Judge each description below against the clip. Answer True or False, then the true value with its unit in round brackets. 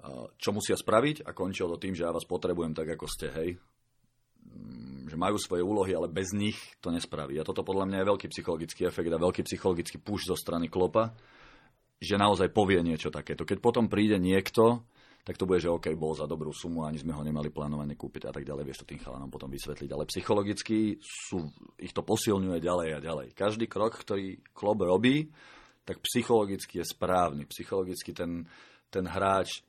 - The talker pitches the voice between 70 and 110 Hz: True (90 Hz)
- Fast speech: True (190 wpm)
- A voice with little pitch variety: False (4.9 semitones)